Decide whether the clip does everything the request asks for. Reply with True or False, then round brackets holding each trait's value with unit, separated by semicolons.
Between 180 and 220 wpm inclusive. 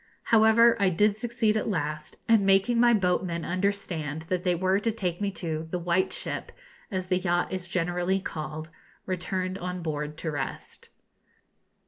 False (160 wpm)